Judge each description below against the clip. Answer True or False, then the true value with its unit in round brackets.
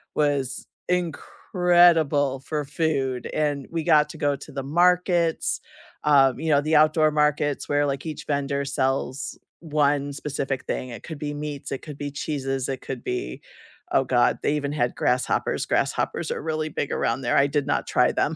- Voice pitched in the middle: True (145 Hz)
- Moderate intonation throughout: False (2.1 semitones)